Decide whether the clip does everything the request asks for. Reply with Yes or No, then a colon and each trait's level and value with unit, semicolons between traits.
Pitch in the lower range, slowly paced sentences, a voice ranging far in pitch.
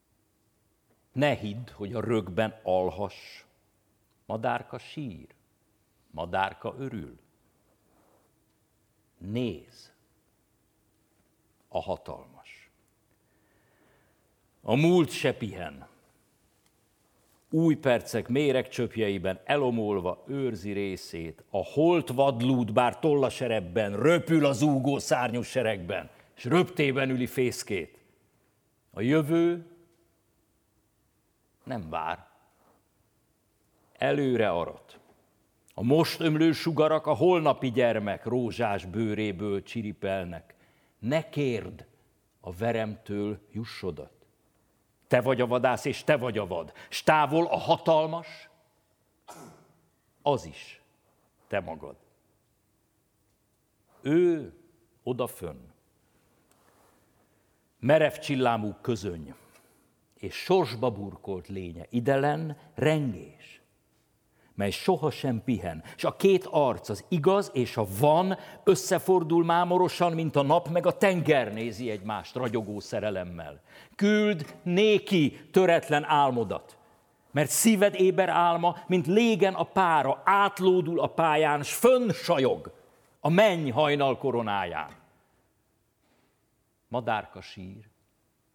Yes: low, 125 Hz; slow, 90 wpm; wide, 7.1 semitones